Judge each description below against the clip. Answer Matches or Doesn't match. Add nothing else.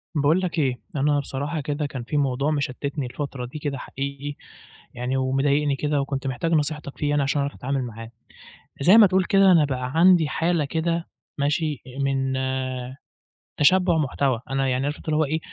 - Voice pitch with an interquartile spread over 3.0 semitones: Doesn't match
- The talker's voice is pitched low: Doesn't match